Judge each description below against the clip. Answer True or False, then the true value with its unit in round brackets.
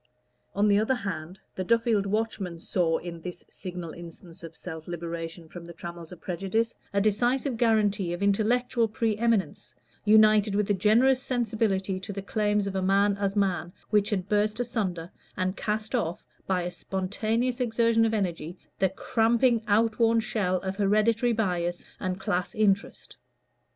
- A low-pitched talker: False (200 Hz)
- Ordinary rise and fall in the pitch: True (3.6 semitones)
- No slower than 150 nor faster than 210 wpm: True (160 wpm)